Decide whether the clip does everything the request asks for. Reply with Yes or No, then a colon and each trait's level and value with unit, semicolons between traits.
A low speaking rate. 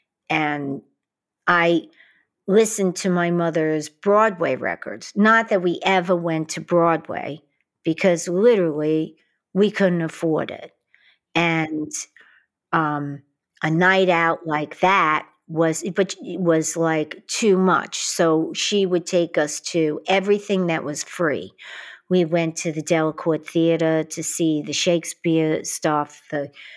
Yes: slow, 130 wpm